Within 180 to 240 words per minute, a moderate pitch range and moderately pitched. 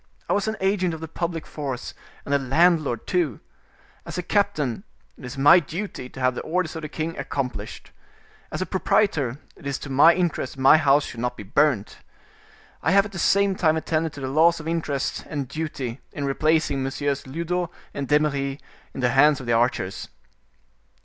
Yes: average, 190 wpm; average, 3.9 semitones; medium, 150 Hz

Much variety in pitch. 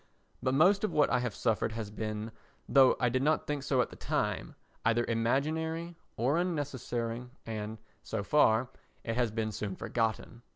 No: average, 4.5 semitones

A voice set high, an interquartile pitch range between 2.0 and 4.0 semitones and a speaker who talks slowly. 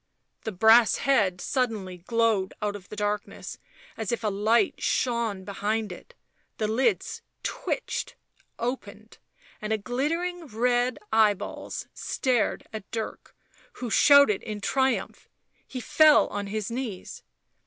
Yes: high, 220 Hz; average, 3.4 semitones; slow, 120 wpm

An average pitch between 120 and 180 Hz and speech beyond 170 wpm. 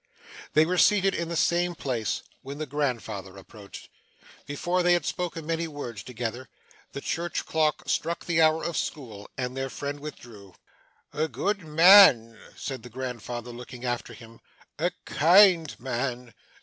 No: medium, 140 Hz; average, 155 wpm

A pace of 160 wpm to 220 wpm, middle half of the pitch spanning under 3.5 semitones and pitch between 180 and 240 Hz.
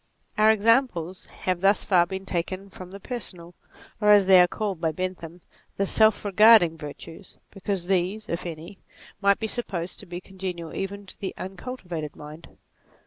Yes: average, 170 wpm; average, 2.7 semitones; medium, 185 Hz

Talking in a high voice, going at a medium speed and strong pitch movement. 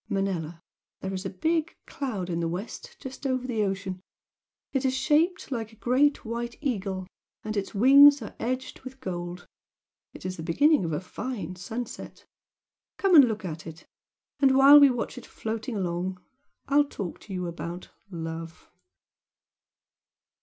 Yes: high, 220 Hz; average, 160 wpm; wide, 6.5 semitones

